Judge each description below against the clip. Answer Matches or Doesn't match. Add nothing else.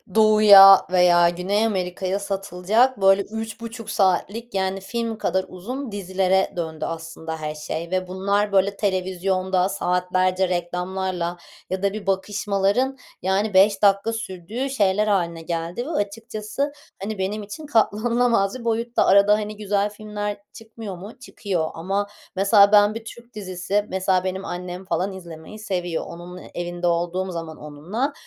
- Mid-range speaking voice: Doesn't match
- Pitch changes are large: Doesn't match